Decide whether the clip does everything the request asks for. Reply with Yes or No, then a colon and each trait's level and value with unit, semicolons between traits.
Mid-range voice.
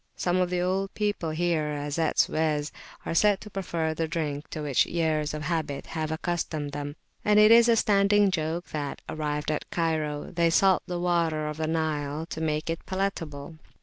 Yes: medium, 160 Hz